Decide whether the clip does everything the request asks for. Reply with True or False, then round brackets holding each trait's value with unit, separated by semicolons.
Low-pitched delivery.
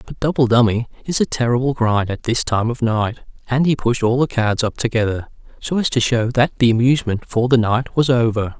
True (120 Hz)